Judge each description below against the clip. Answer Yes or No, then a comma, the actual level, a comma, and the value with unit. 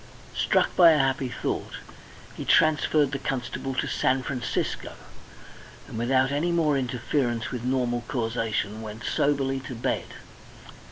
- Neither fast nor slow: No, slow, 130 wpm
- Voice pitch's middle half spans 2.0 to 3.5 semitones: Yes, average, 2.7 semitones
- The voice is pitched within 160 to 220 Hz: No, low, 130 Hz